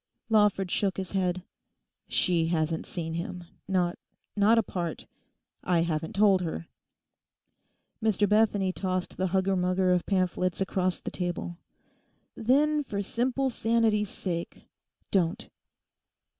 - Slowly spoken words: Yes, slow, 115 wpm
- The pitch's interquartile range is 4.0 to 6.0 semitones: No, average, 2.9 semitones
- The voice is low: No, medium, 185 Hz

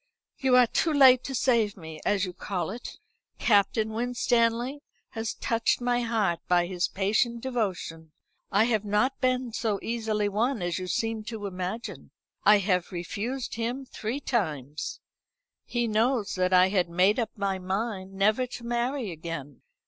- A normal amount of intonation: Yes, average, 4.3 semitones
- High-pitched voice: Yes, high, 215 Hz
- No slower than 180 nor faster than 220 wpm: No, average, 155 wpm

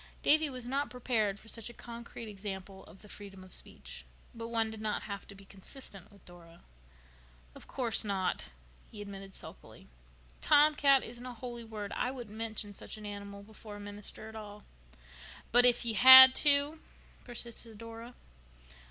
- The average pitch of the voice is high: Yes, high, 220 Hz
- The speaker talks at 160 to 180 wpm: Yes, average, 170 wpm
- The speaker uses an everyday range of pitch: Yes, average, 3.1 semitones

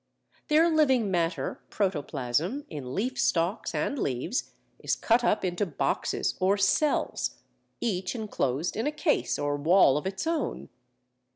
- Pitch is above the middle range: Yes, high, 195 Hz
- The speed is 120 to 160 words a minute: Yes, slow, 135 wpm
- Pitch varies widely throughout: Yes, wide, 7.8 semitones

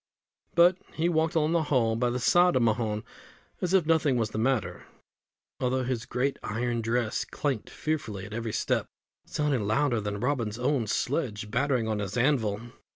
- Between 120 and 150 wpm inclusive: No, average, 170 wpm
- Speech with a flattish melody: No, average, 4.8 semitones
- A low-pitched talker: Yes, low, 125 Hz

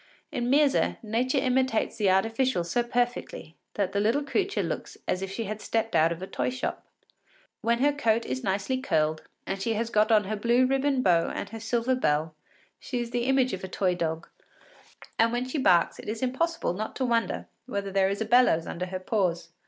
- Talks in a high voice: Yes, high, 225 Hz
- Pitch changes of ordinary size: Yes, average, 4.9 semitones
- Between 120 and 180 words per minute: No, fast, 205 wpm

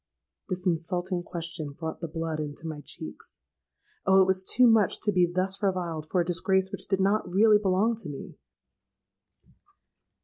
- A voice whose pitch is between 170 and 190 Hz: Yes, medium, 185 Hz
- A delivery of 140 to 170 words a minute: Yes, average, 165 wpm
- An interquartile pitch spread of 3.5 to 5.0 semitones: No, average, 2.7 semitones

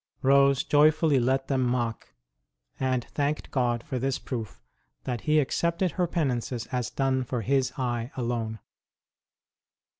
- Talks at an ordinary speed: No, slow, 130 wpm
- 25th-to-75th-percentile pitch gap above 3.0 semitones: No, narrow, 2.6 semitones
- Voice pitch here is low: Yes, low, 130 Hz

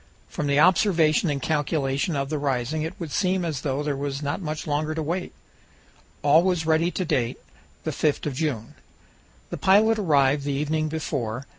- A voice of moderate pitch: Yes, medium, 150 Hz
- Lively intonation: No, narrow, 2.6 semitones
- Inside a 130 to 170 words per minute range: No, average, 180 wpm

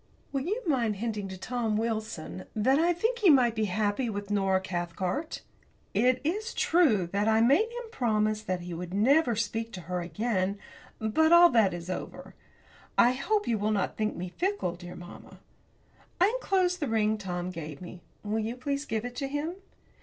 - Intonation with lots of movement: Yes, wide, 6.9 semitones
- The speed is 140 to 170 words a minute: No, average, 185 wpm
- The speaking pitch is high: Yes, high, 220 Hz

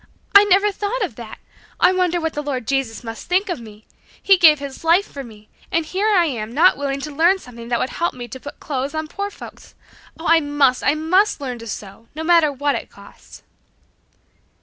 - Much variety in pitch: Yes, wide, 5.9 semitones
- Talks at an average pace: No, fast, 220 wpm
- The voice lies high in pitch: Yes, very high, 295 Hz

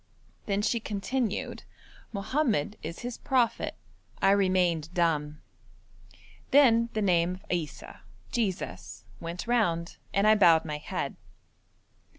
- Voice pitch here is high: Yes, high, 195 Hz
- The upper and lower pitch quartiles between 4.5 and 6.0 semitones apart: Yes, average, 5.2 semitones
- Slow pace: Yes, slow, 115 wpm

